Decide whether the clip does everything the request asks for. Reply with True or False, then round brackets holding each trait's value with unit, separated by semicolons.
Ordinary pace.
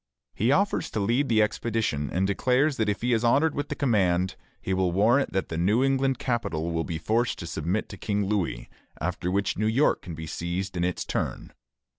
False (210 wpm)